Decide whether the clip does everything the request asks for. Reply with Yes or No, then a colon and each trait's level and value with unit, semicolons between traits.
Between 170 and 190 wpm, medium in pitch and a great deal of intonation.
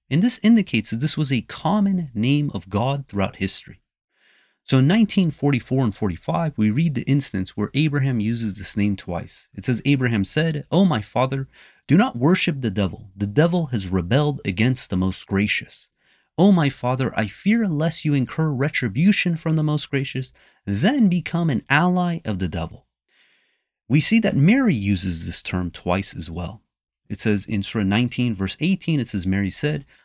No: average, 180 wpm; low, 130 Hz; wide, 7.7 semitones